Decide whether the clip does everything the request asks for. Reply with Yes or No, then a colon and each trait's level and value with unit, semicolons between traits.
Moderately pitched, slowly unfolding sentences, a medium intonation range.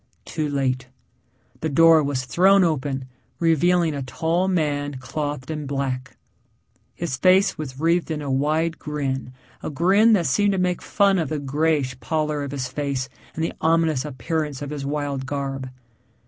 No: medium, 150 Hz; average, 160 wpm; average, 3.4 semitones